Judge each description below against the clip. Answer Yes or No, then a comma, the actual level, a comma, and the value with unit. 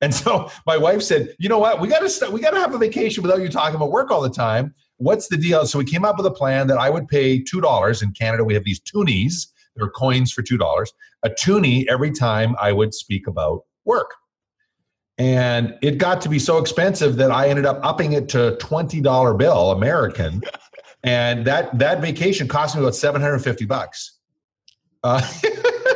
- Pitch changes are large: Yes, wide, 6.6 semitones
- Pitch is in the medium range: Yes, medium, 145 Hz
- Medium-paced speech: No, fast, 210 wpm